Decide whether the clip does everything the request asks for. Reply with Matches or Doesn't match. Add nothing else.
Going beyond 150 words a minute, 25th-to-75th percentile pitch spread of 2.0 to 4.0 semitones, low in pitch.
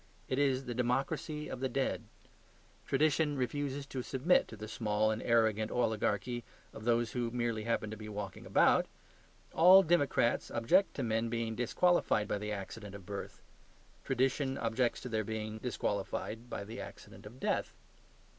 Matches